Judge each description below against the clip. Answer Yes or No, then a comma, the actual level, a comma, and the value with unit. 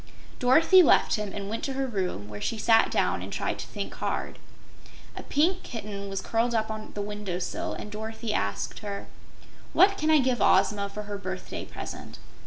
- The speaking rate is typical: Yes, average, 195 wpm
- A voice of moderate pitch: No, high, 210 Hz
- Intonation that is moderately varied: Yes, average, 3.7 semitones